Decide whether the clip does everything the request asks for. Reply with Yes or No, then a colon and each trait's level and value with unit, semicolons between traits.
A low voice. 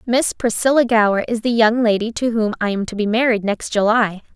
No: high, 225 Hz